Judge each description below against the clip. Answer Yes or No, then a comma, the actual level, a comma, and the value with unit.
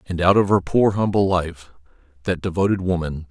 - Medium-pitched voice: No, very low, 90 Hz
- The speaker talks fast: No, average, 180 wpm